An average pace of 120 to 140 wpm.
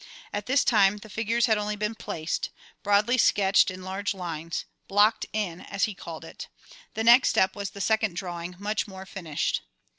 No: average, 180 wpm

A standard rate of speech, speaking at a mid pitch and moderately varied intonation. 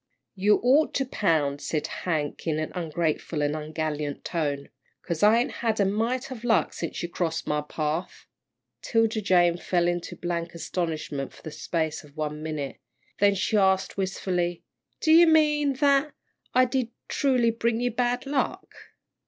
No: average, 160 wpm; medium, 180 Hz; wide, 6.9 semitones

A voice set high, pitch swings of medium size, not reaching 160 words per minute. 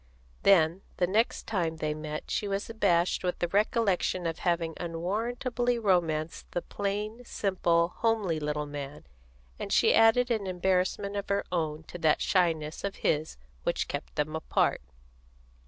No: medium, 180 Hz; average, 4.2 semitones; average, 150 wpm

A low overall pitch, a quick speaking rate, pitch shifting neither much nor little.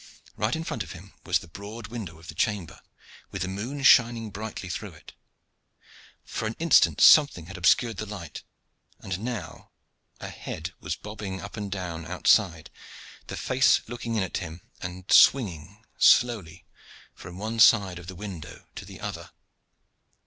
No: low, 100 Hz; average, 165 wpm; average, 4.1 semitones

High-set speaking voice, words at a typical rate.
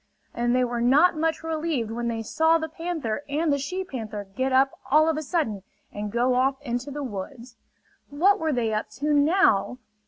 Yes: very high, 270 Hz; average, 195 wpm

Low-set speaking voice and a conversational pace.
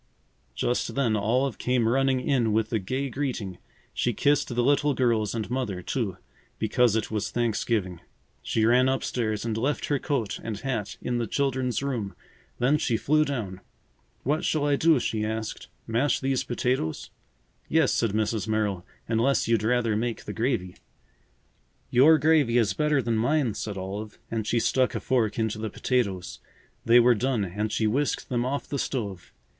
Yes: low, 120 Hz; average, 170 wpm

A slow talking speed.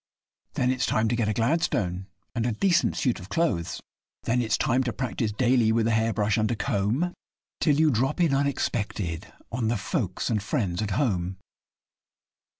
No: average, 180 wpm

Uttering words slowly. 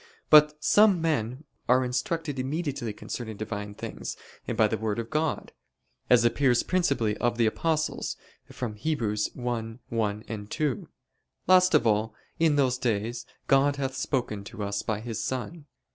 No: average, 145 wpm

